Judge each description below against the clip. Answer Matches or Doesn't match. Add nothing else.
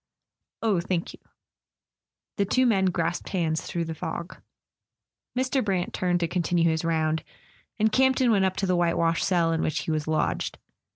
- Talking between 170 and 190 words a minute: Matches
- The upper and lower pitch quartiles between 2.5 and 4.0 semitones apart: Matches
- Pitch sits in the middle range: Matches